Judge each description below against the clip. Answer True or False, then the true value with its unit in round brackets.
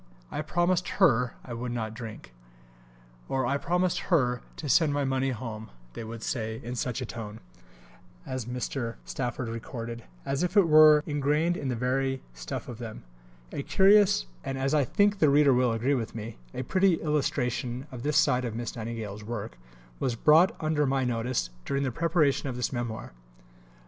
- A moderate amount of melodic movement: True (4.3 semitones)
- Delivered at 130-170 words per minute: False (180 wpm)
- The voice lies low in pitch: True (130 Hz)